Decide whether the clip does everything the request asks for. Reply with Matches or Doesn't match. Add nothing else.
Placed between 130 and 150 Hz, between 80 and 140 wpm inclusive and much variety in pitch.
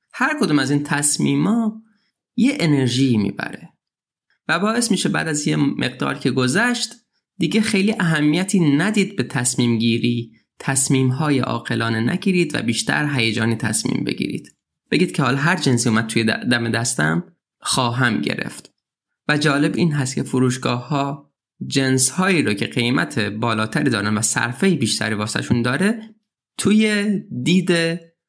Matches